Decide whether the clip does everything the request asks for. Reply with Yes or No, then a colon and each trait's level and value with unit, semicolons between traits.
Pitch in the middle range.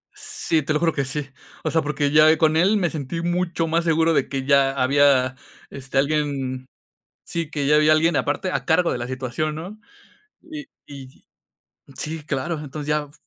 Yes: medium, 150 Hz